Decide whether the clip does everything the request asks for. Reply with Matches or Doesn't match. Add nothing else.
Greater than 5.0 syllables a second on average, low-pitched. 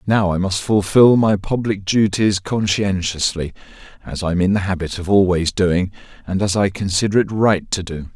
Doesn't match